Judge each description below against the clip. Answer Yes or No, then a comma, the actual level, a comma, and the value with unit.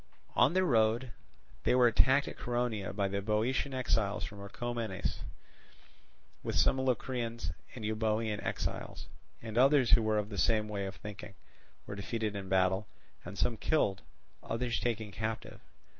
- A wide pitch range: No, average, 3.1 semitones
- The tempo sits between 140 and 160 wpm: Yes, average, 150 wpm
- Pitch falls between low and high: No, low, 110 Hz